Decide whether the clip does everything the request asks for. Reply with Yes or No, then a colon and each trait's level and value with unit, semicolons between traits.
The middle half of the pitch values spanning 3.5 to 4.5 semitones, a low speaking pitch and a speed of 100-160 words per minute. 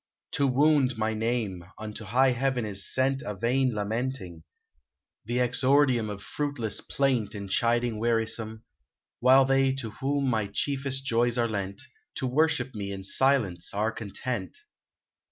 Yes: average, 3.8 semitones; low, 120 Hz; average, 155 wpm